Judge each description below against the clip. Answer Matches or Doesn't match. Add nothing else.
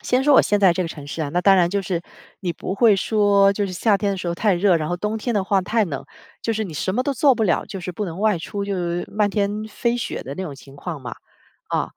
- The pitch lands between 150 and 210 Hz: Matches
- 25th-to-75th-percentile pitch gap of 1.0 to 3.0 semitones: Doesn't match